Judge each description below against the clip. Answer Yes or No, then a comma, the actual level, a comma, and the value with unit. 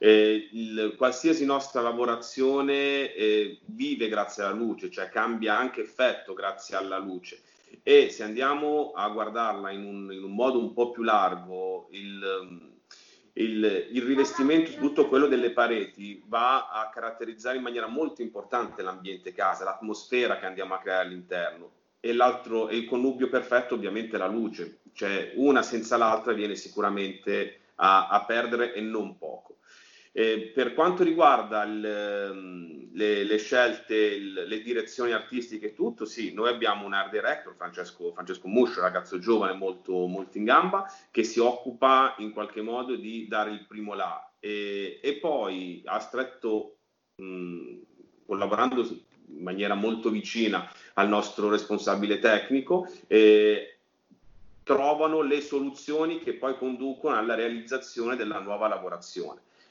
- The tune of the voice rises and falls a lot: No, average, 4.5 semitones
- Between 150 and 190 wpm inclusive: No, average, 140 wpm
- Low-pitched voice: Yes, low, 115 Hz